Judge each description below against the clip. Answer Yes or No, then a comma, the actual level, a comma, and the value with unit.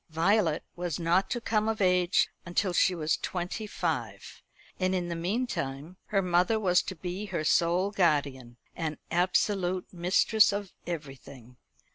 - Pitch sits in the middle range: Yes, medium, 180 Hz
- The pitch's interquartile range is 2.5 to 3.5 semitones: Yes, average, 2.9 semitones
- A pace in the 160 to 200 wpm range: No, average, 145 wpm